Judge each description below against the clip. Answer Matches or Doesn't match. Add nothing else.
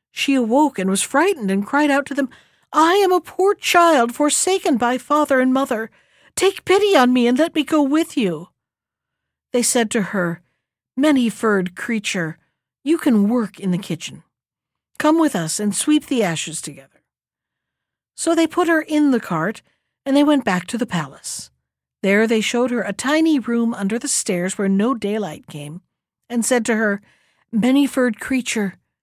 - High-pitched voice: Matches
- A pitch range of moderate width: Doesn't match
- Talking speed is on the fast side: Doesn't match